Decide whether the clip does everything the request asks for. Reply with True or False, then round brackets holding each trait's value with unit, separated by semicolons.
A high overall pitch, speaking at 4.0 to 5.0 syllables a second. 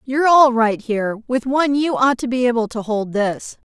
False (240 Hz; 5.2 syllables/s)